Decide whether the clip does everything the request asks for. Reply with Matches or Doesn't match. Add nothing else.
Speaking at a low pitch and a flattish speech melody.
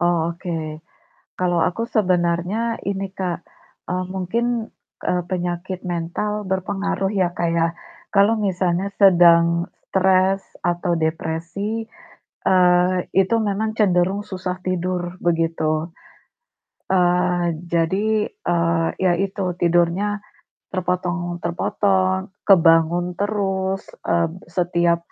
Doesn't match